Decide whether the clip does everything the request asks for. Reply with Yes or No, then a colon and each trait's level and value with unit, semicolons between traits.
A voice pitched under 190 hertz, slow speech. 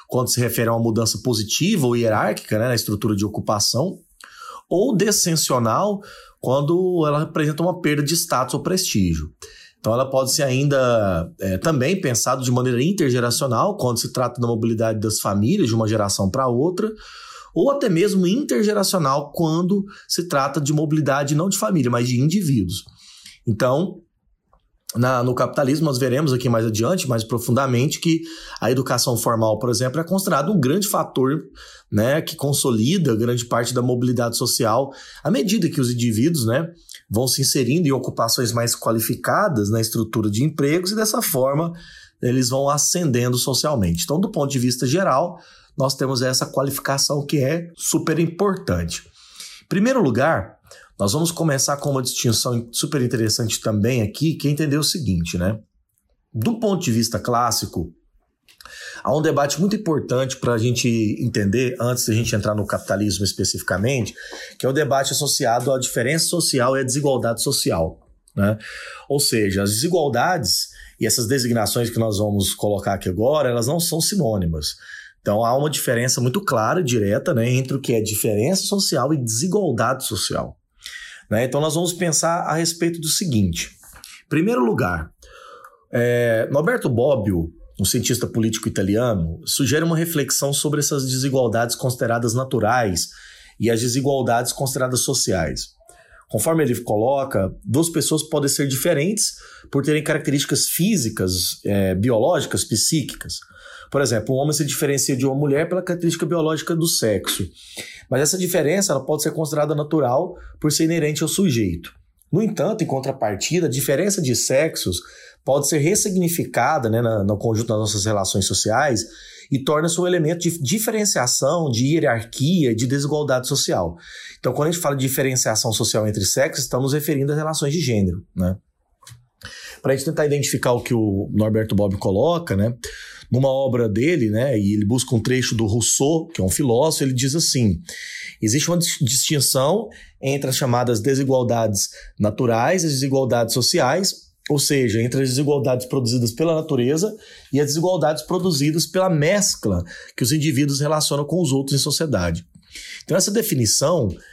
No: low, 135 Hz; average, 160 wpm